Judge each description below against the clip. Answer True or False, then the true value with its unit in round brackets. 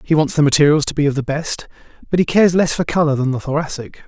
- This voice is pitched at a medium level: True (150 Hz)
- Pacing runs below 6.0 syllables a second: False (6.8 syllables/s)